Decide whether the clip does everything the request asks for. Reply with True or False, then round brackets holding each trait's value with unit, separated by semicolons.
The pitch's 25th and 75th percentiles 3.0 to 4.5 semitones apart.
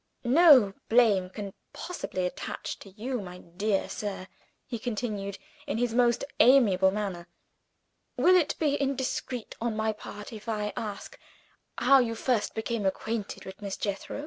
True (3.7 semitones)